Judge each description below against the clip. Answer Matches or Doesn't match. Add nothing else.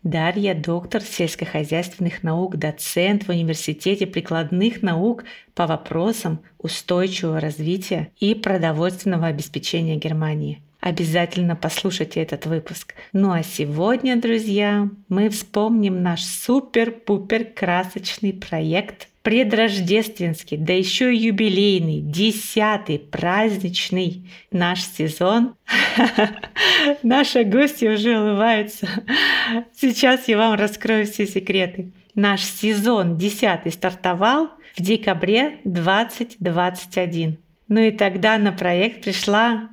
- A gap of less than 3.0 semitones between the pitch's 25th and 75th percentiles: Doesn't match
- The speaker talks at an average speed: Doesn't match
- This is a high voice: Matches